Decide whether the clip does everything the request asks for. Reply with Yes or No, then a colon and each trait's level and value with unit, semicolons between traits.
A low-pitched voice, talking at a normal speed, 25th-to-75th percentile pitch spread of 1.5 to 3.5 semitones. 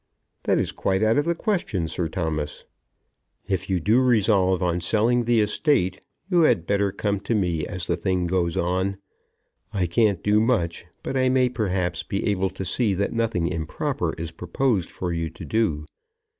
No: very low, 95 Hz; average, 180 wpm; average, 4.4 semitones